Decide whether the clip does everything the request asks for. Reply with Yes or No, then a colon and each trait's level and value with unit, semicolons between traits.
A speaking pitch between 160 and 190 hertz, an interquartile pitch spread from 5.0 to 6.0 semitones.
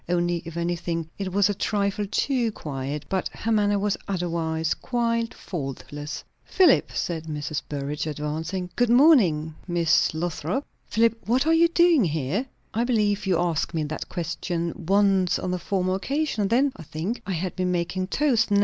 Yes: medium, 185 Hz; wide, 5.4 semitones